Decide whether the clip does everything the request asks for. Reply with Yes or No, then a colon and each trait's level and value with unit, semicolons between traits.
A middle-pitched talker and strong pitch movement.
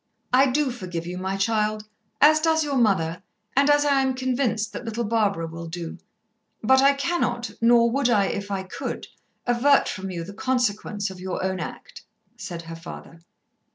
No: high, 220 Hz; wide, 5.7 semitones